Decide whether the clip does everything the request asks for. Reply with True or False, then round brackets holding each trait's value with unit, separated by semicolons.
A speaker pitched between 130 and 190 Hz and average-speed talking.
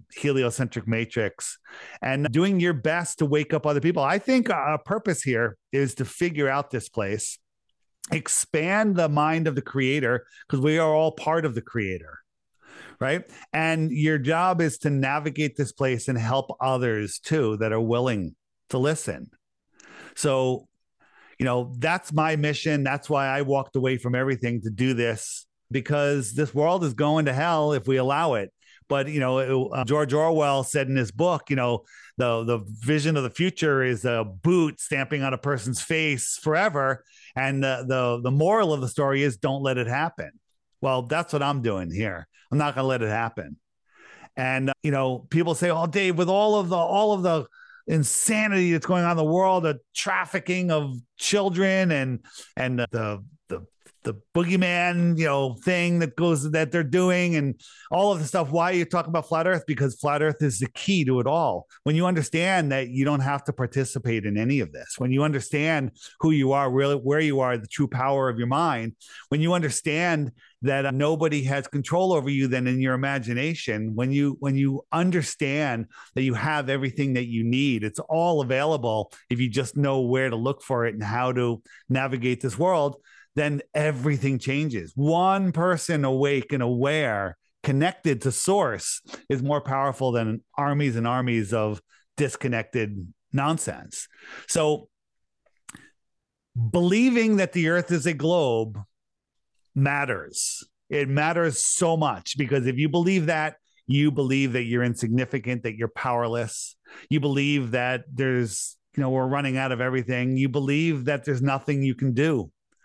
True (140 Hz; 180 wpm)